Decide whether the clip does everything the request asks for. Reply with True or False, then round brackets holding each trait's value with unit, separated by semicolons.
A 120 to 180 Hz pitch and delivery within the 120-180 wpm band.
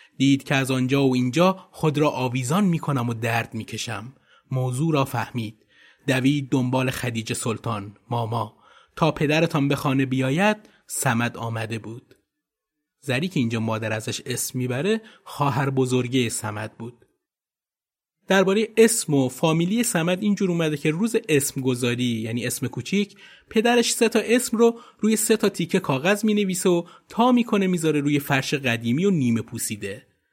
True (135 Hz; 155 wpm)